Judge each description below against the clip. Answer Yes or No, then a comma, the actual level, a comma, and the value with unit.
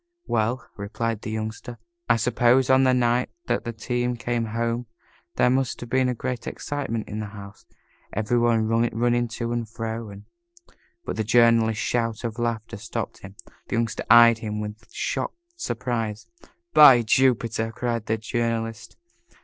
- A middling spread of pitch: No, narrow, 1.6 semitones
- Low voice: Yes, low, 115 Hz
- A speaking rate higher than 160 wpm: No, average, 155 wpm